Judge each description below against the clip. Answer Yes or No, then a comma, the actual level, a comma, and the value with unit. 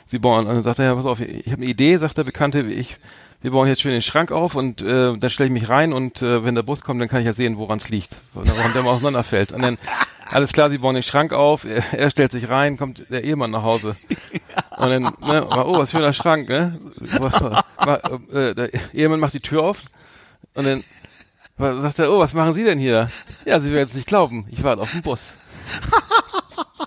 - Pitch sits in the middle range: No, low, 130 Hz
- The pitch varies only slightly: No, average, 3.3 semitones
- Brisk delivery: Yes, fast, 240 wpm